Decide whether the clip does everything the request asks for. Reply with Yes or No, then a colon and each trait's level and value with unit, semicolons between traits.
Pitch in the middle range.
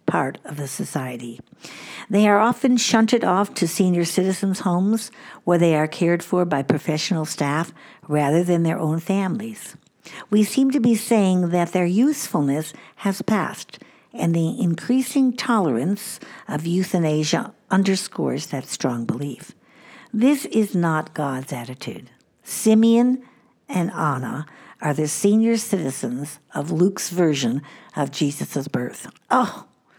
Yes: medium, 180 Hz